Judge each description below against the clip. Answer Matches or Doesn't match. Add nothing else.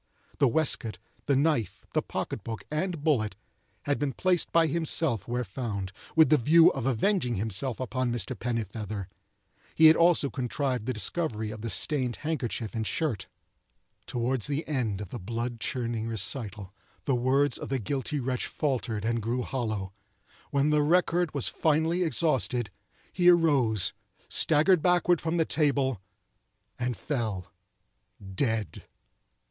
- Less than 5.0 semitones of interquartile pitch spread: Doesn't match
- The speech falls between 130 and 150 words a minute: Matches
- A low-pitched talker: Matches